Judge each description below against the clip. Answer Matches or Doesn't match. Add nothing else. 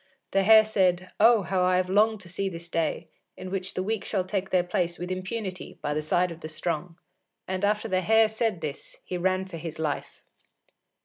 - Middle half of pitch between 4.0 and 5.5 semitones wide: Doesn't match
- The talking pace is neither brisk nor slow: Doesn't match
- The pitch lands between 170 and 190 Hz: Matches